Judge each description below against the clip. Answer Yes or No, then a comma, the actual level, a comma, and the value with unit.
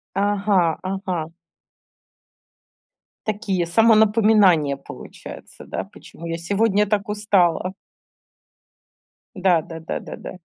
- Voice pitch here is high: Yes, high, 195 Hz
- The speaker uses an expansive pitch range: No, average, 3.5 semitones